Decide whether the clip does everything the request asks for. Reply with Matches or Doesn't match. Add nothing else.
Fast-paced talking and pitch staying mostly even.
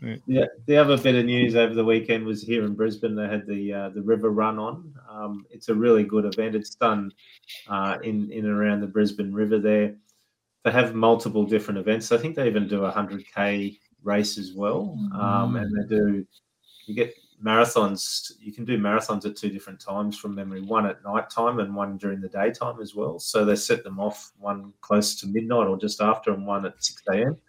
Matches